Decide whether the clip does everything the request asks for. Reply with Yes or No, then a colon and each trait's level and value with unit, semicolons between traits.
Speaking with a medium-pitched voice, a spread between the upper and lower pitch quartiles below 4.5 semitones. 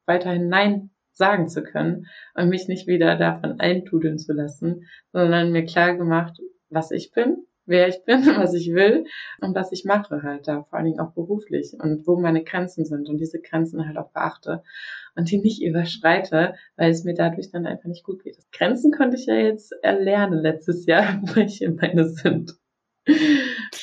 Yes: medium, 175 Hz; average, 3.1 semitones